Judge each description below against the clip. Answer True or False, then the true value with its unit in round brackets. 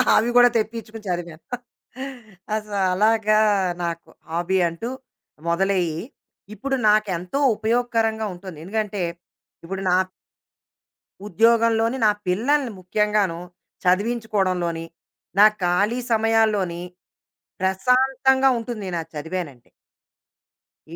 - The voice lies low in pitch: False (210 Hz)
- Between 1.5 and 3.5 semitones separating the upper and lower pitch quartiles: False (4.0 semitones)